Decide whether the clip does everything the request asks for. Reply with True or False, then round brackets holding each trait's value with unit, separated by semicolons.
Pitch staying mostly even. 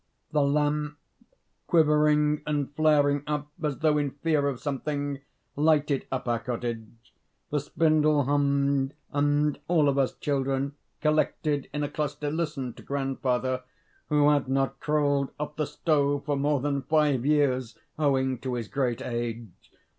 True (1.9 semitones)